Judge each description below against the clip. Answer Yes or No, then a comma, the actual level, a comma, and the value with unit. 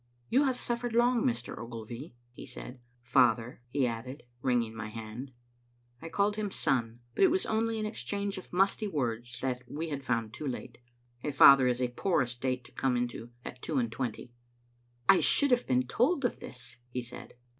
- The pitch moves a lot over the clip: Yes, wide, 8.6 semitones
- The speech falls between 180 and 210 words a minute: Yes, average, 190 wpm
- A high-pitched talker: No, low, 130 Hz